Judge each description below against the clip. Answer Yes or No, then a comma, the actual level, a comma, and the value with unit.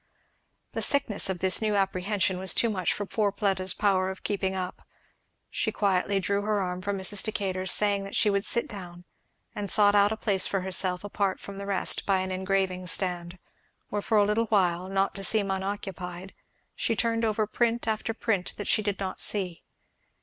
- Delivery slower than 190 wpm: No, average, 195 wpm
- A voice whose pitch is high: Yes, high, 195 Hz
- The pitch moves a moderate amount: No, narrow, 1.8 semitones